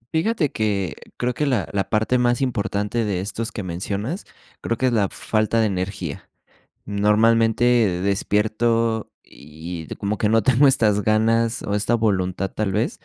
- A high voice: No, low, 110 Hz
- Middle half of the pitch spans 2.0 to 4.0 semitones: Yes, average, 2.8 semitones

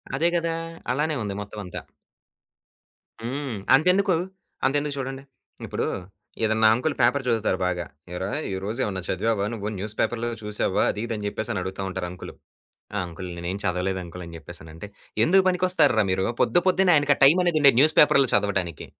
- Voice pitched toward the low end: Yes, low, 110 Hz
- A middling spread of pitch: No, wide, 7.4 semitones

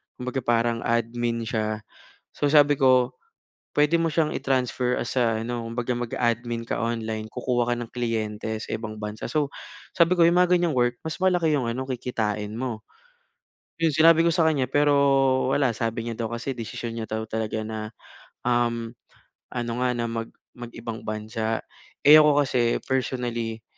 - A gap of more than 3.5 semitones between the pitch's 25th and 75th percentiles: No, average, 2.8 semitones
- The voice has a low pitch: Yes, low, 120 Hz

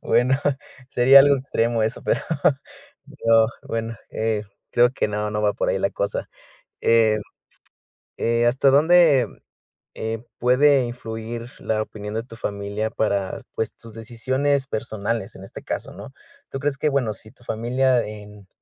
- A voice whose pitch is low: Yes, low, 115 Hz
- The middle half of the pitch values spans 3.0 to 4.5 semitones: Yes, average, 3.3 semitones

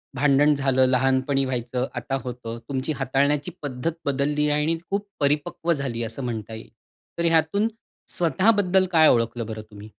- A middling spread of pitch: Yes, average, 3.5 semitones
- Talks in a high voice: No, low, 135 Hz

